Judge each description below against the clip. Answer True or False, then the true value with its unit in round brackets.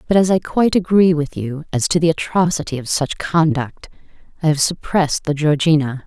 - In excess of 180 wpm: True (190 wpm)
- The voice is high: False (155 Hz)